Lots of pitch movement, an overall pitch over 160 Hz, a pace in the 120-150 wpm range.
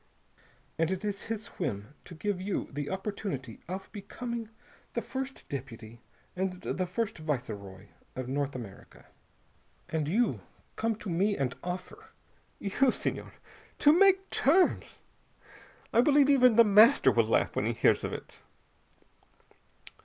Yes: wide, 8.4 semitones; high, 190 Hz; average, 140 wpm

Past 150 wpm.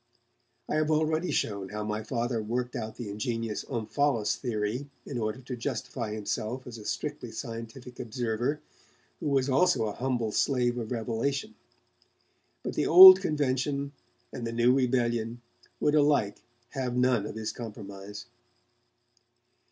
No: average, 140 wpm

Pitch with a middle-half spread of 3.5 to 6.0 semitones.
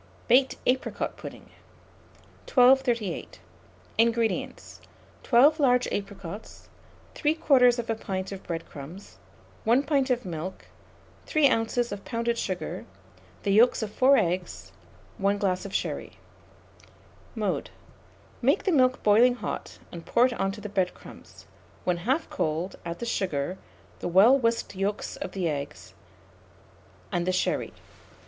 Yes: average, 5.1 semitones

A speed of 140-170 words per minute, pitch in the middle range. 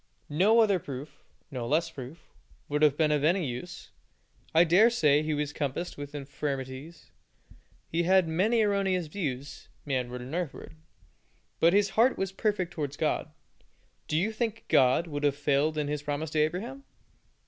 Yes: average, 160 wpm; medium, 155 Hz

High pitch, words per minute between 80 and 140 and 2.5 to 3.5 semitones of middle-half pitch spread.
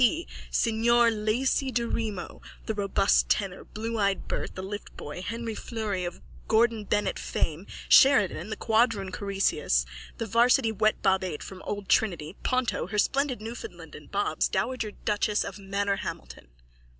Yes: high, 215 Hz; slow, 135 wpm; average, 2.9 semitones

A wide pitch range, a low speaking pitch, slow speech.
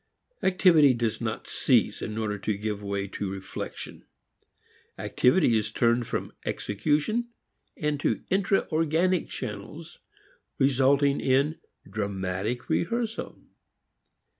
Yes: wide, 7.1 semitones; low, 130 Hz; slow, 100 wpm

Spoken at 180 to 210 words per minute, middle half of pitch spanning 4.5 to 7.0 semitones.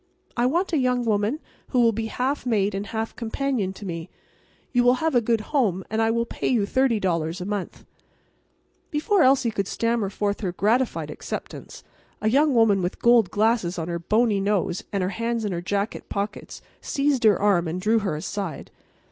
No: average, 190 wpm; average, 3.8 semitones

